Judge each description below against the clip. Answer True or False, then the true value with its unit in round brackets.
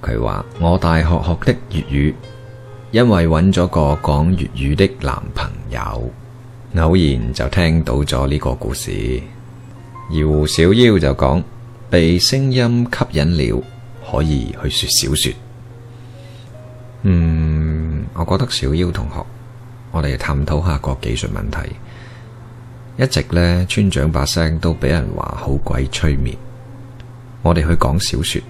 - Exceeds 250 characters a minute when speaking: False (185 characters per minute)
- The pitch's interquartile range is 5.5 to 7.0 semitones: False (7.7 semitones)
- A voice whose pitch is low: True (90 Hz)